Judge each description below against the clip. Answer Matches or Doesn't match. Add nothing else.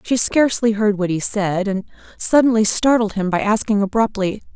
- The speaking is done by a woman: Matches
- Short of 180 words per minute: Matches